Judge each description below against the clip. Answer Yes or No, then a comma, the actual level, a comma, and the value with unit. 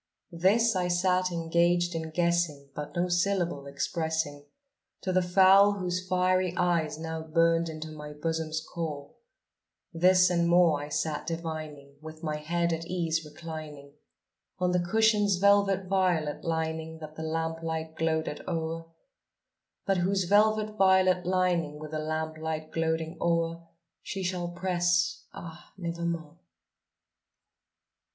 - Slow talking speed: Yes, slow, 130 wpm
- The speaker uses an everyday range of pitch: No, narrow, 2.3 semitones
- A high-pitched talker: No, medium, 170 Hz